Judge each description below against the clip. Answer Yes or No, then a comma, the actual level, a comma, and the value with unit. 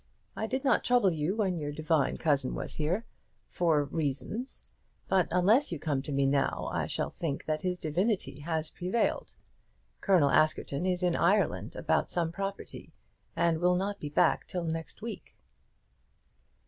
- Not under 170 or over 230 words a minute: No, average, 160 wpm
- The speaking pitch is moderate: Yes, medium, 170 Hz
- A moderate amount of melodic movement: Yes, average, 4.0 semitones